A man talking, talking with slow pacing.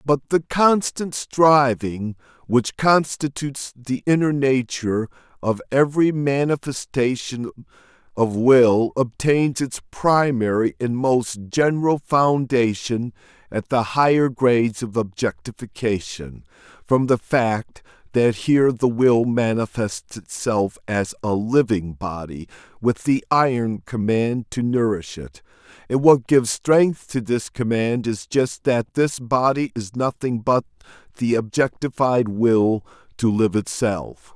Yes: male; slow, 120 wpm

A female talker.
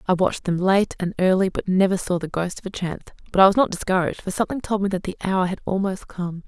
Yes: female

